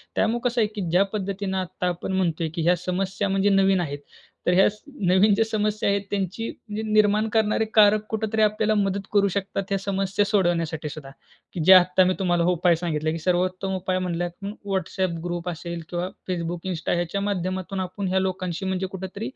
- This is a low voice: No, high, 190 Hz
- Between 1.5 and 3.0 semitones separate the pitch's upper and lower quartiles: Yes, narrow, 2.5 semitones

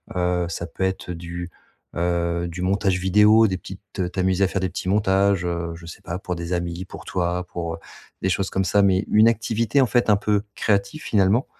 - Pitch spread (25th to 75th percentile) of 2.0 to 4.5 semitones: Yes, narrow, 2.5 semitones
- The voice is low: Yes, very low, 95 Hz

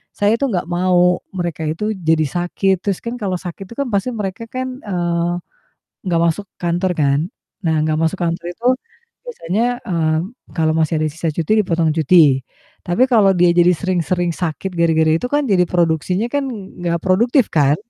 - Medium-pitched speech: Yes, medium, 175 Hz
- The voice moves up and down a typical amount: Yes, average, 3.7 semitones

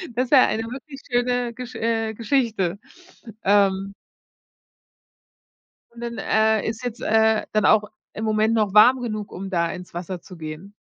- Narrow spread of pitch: No, average, 3.3 semitones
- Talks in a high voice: Yes, high, 220 Hz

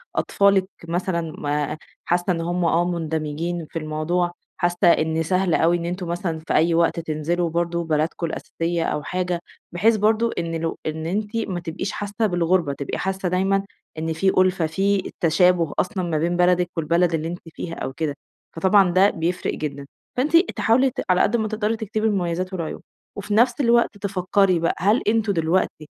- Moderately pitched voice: Yes, medium, 175 Hz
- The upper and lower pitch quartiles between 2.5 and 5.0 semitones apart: Yes, average, 3.0 semitones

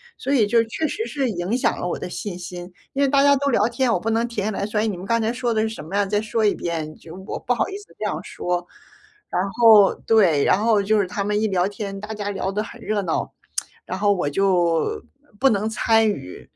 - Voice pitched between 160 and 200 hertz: No, high, 210 Hz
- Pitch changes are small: No, average, 3.4 semitones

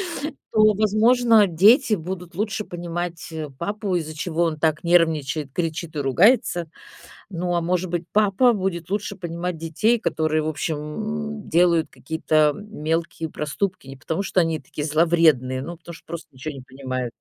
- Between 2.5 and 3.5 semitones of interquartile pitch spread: No, average, 4.1 semitones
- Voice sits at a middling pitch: Yes, medium, 170 Hz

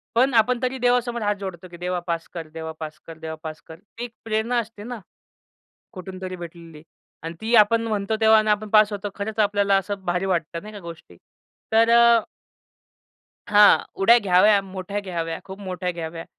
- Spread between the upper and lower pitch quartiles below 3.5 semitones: No, average, 4.1 semitones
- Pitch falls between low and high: No, high, 200 Hz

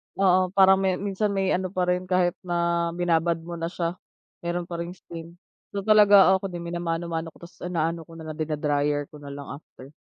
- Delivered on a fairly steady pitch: Yes, narrow, 2.0 semitones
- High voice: No, medium, 170 Hz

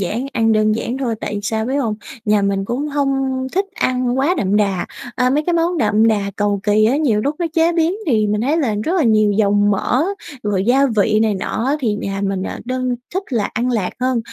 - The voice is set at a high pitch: Yes, high, 230 Hz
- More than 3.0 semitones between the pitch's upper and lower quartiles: Yes, average, 4.6 semitones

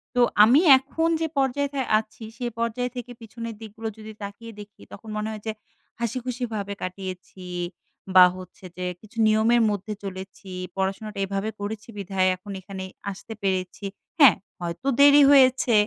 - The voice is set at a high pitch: Yes, high, 215 Hz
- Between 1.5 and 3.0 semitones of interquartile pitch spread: No, average, 3.8 semitones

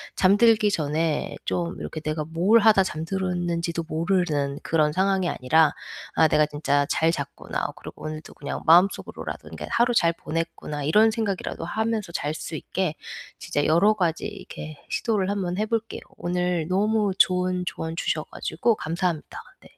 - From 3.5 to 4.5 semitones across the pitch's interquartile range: Yes, average, 3.9 semitones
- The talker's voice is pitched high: No, medium, 175 Hz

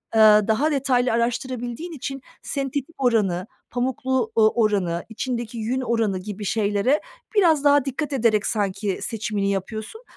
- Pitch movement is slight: No, average, 3.7 semitones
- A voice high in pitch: Yes, high, 230 Hz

